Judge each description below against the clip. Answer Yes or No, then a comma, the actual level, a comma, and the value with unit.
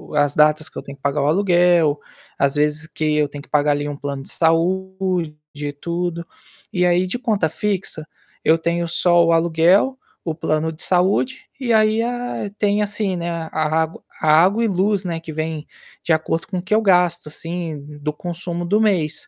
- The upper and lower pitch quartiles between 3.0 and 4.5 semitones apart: Yes, average, 3.4 semitones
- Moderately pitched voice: Yes, medium, 170 Hz